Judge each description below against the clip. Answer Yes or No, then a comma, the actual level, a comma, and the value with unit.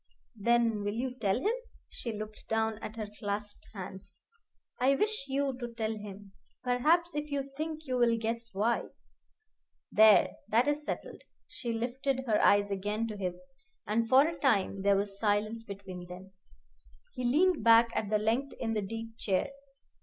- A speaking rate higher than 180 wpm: No, average, 165 wpm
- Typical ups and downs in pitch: Yes, average, 4.0 semitones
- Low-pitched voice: No, high, 225 Hz